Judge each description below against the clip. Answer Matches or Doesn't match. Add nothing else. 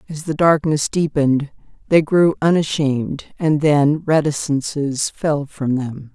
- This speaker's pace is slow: Matches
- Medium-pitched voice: Matches